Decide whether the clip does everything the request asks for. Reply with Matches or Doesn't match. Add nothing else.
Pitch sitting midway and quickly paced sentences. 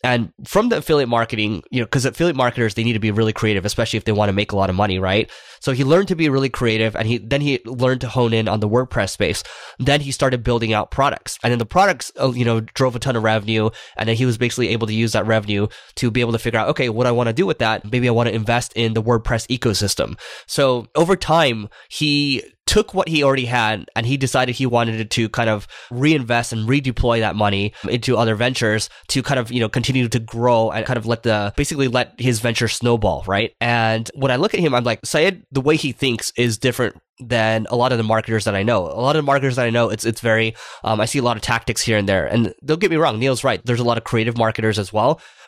Doesn't match